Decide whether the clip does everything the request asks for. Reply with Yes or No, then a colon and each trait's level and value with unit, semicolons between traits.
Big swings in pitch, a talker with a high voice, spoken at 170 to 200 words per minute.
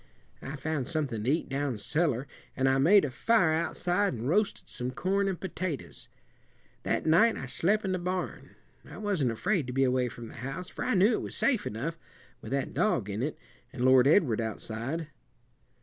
No: wide, 6.5 semitones; medium, 150 Hz; average, 195 wpm